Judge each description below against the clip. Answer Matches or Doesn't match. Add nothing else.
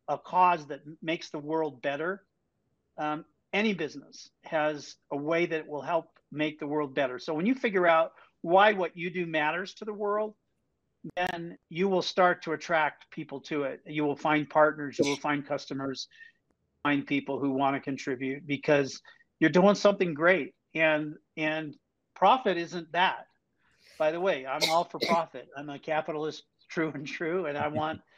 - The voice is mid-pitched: Matches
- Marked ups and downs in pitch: Doesn't match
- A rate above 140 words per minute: Matches